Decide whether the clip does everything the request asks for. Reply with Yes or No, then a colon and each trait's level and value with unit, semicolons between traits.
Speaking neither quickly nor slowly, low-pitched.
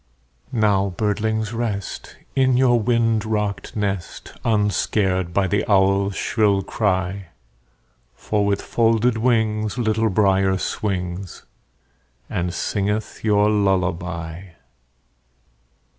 No: slow, 95 wpm; low, 105 Hz